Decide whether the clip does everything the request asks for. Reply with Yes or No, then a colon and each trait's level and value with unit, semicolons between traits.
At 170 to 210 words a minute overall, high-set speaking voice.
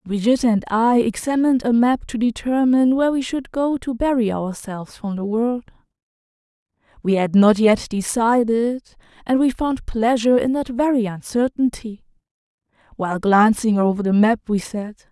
No: average, 150 wpm; high, 230 Hz